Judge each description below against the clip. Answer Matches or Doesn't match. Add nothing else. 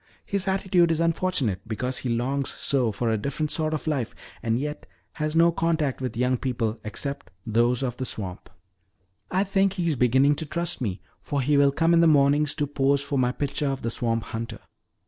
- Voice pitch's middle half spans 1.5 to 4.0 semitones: Doesn't match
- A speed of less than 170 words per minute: Doesn't match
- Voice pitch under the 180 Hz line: Matches